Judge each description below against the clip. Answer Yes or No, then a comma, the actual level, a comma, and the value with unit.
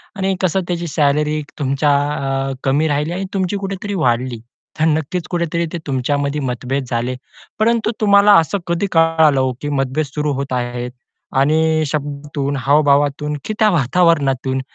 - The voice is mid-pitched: Yes, medium, 150 Hz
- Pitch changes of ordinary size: Yes, average, 4.0 semitones